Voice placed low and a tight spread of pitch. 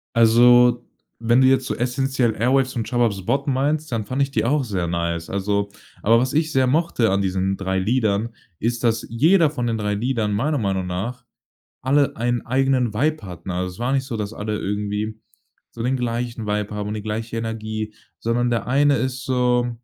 No: low, 115 Hz; average, 3.7 semitones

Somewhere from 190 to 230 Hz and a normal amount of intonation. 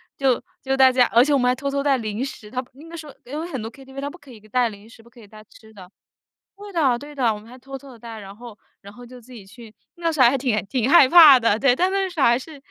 No: very high, 255 Hz; average, 3.6 semitones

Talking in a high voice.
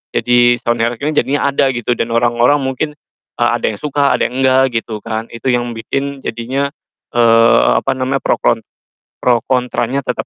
No: low, 120 Hz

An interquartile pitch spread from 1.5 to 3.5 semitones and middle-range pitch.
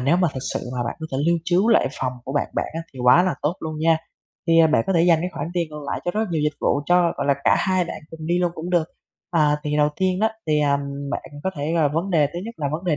Yes: average, 3.0 semitones; medium, 165 Hz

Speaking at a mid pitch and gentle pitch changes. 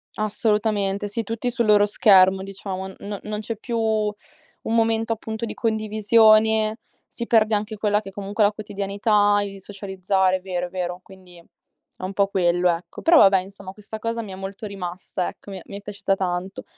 No: high, 205 Hz; narrow, 2.1 semitones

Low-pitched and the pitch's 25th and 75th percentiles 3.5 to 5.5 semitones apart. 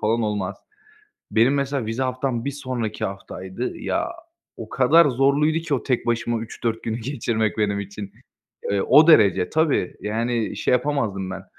Yes: low, 115 Hz; average, 4.6 semitones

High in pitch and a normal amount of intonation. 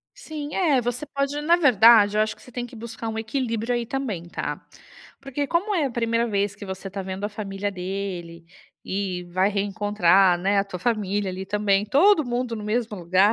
Yes: high, 215 Hz; average, 4.1 semitones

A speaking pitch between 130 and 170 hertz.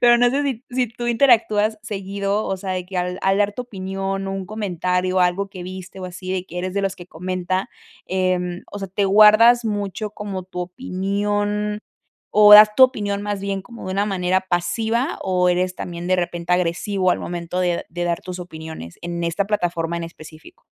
No: high, 190 Hz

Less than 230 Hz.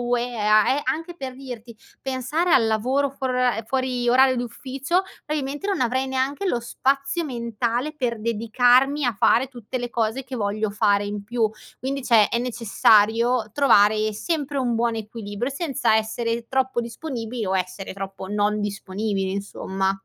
No: high, 240 Hz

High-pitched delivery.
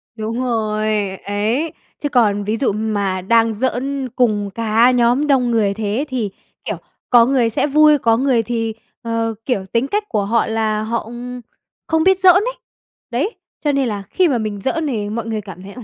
Yes: high, 230 Hz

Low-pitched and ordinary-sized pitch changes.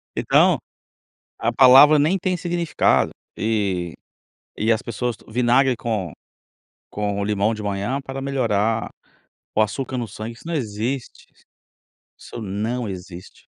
Yes: low, 115 Hz; average, 4.4 semitones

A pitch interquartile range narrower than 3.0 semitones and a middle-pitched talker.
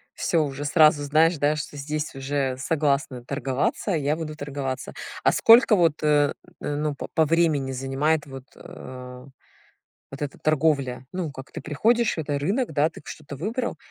Yes: narrow, 2.5 semitones; medium, 145 Hz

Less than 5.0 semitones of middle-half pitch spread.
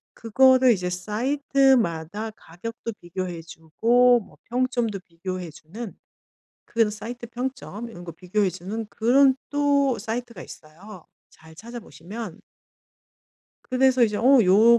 No: average, 5.3 semitones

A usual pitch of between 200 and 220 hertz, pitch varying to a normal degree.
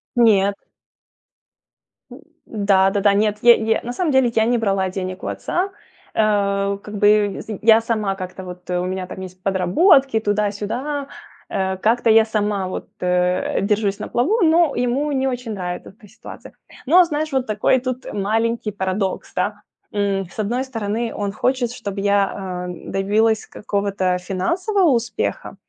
Yes: high, 210 Hz; average, 3.7 semitones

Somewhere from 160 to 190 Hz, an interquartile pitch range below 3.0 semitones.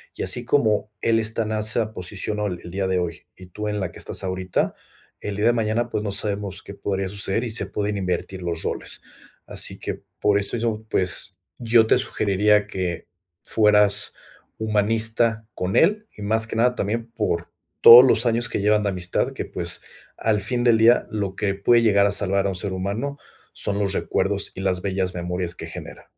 No: low, 105 Hz; narrow, 2.6 semitones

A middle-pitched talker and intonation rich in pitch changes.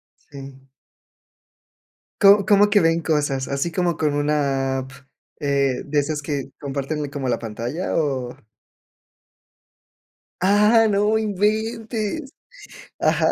Yes: medium, 150 Hz; wide, 6.7 semitones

